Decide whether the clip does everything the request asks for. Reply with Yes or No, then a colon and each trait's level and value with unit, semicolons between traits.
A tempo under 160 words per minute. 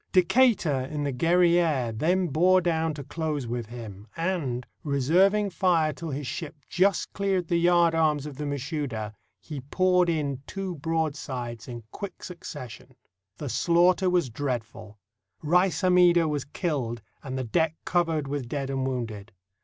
Yes: average, 145 wpm